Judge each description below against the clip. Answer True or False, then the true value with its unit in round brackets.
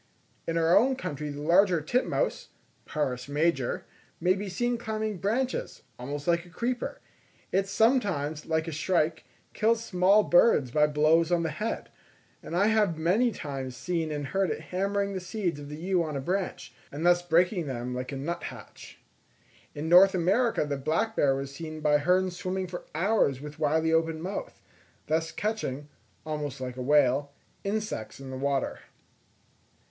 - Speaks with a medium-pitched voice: True (165 Hz)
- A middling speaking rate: True (165 wpm)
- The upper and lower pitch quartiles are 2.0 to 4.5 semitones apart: False (5.0 semitones)